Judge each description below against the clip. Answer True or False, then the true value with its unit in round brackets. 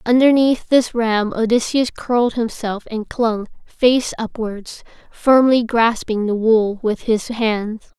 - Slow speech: True (130 wpm)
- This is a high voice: True (230 Hz)